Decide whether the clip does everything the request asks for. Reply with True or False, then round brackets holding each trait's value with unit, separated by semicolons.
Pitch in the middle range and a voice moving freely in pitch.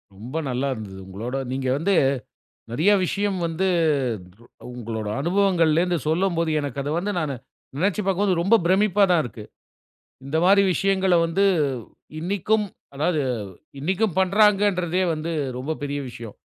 True (170 Hz; 5.8 semitones)